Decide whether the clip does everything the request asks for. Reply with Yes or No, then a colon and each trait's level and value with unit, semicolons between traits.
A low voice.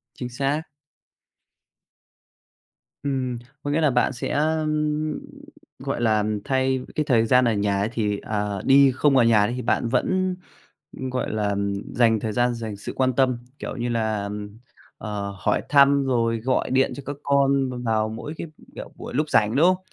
Yes: low, 125 Hz